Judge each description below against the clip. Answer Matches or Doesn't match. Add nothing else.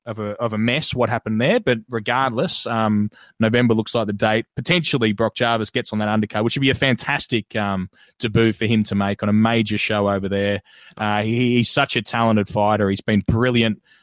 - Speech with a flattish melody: Matches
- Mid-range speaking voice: Doesn't match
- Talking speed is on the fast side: Matches